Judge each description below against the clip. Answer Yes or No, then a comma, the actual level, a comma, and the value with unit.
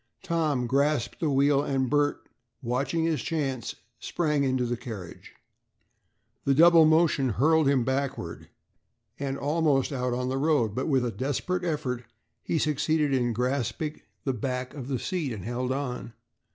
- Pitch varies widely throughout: No, average, 3.3 semitones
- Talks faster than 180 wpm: No, average, 150 wpm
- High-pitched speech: No, low, 135 Hz